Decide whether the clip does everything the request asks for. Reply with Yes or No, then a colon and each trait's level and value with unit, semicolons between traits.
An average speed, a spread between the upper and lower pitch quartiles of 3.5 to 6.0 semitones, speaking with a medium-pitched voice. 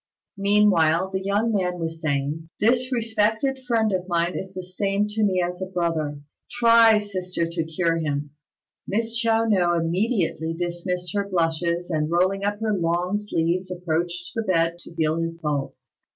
Yes: average, 165 wpm; average, 3.8 semitones; medium, 180 Hz